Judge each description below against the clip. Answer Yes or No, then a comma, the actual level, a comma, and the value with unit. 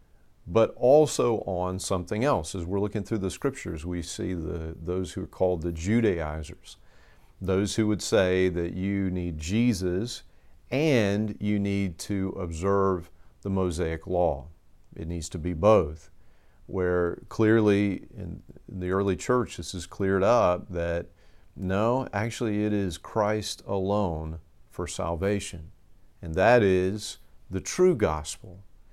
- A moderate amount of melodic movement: Yes, average, 3.3 semitones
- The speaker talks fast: No, slow, 135 wpm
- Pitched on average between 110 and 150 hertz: No, very low, 95 Hz